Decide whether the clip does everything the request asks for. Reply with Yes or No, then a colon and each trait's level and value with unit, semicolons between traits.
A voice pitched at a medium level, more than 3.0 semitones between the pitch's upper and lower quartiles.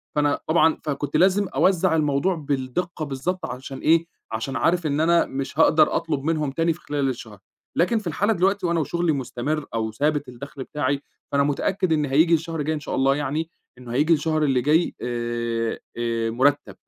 Yes: medium, 150 Hz; average, 3.6 semitones